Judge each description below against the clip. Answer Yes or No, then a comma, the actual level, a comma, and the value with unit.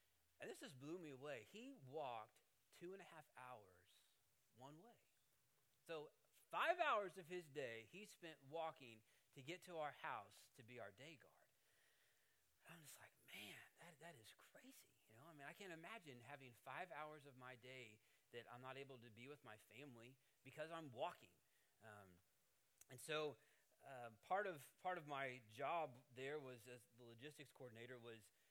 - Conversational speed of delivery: Yes, average, 180 wpm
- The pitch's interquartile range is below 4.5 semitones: No, average, 5.2 semitones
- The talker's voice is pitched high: No, low, 135 Hz